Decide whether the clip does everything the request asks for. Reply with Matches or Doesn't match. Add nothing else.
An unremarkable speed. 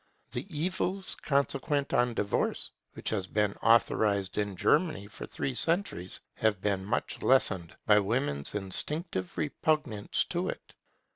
Doesn't match